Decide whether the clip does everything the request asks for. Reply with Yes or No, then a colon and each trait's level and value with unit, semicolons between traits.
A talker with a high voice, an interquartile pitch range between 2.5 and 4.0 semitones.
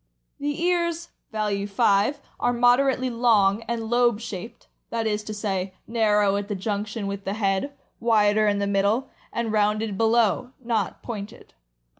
Yes: high, 215 Hz; average, 2.9 semitones